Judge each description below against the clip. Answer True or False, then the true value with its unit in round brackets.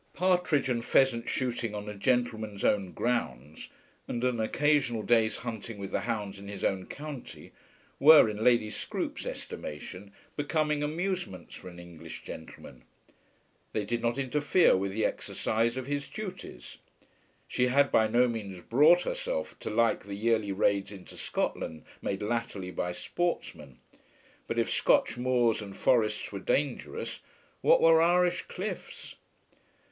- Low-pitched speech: True (115 Hz)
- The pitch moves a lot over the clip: True (6.0 semitones)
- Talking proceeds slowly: False (145 wpm)